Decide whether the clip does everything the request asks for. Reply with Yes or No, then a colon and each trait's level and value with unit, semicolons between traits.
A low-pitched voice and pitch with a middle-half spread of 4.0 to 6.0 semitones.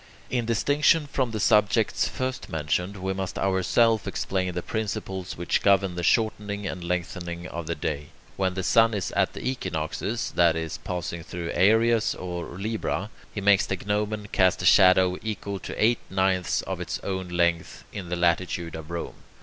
No: very low, 95 Hz; average, 3.4 semitones